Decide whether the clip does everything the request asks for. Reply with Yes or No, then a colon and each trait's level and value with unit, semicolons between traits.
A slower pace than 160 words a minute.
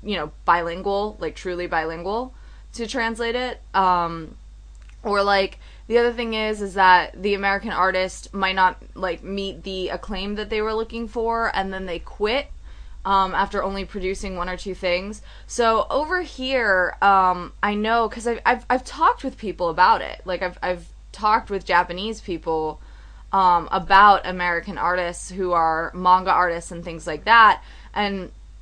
No: average, 165 wpm